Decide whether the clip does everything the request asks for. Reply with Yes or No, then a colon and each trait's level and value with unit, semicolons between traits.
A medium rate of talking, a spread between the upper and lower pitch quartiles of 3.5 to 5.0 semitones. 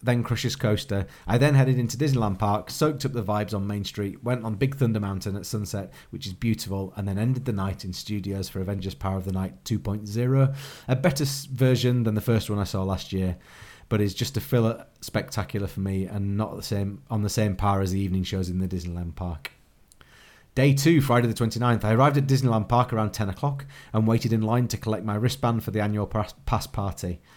No: fast, 220 wpm; average, 3.8 semitones